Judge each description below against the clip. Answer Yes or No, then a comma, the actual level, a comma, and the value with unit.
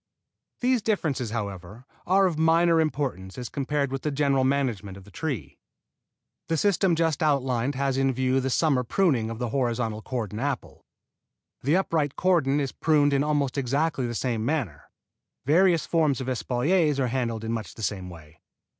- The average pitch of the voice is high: No, low, 135 Hz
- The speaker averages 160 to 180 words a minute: Yes, average, 170 wpm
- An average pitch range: Yes, average, 4.7 semitones